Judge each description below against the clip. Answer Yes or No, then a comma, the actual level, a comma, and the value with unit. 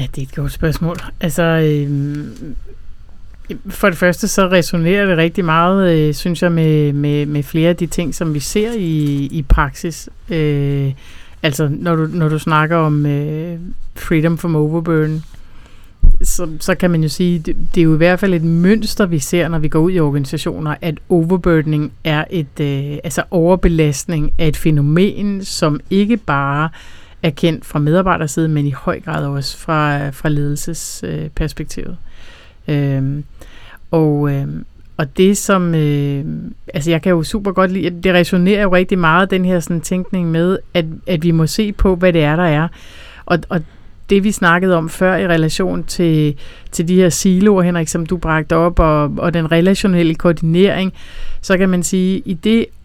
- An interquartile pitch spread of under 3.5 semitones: Yes, average, 3.1 semitones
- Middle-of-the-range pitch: Yes, medium, 165 Hz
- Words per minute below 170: No, average, 180 wpm